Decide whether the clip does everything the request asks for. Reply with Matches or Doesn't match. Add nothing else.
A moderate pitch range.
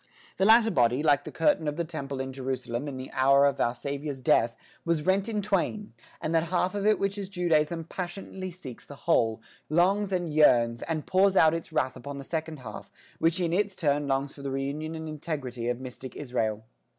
Matches